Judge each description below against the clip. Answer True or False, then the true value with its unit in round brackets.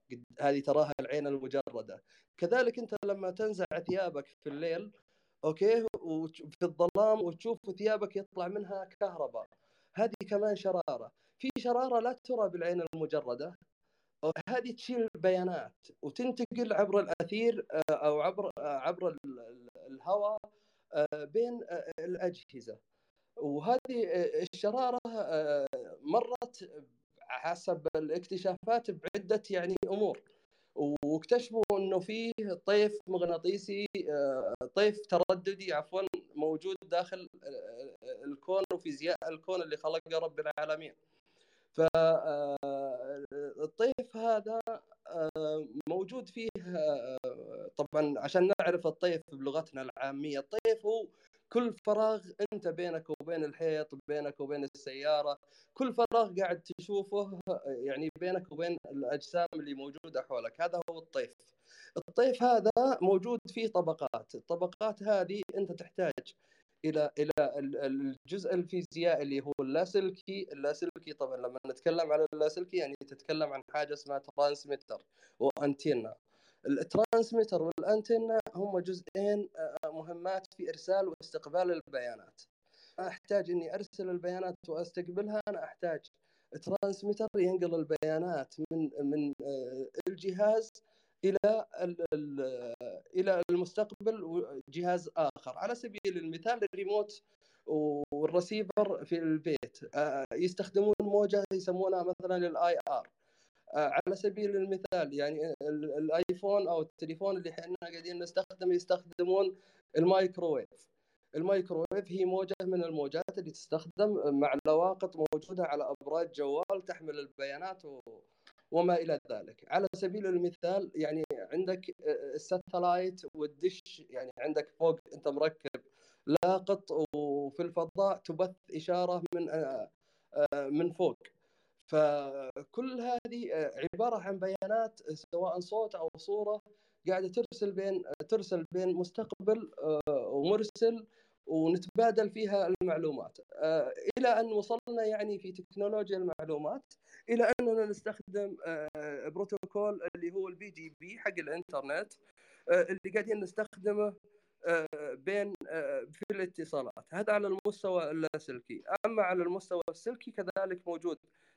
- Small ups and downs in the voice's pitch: False (4.9 semitones)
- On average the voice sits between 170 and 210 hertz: True (185 Hz)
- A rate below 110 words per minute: True (100 wpm)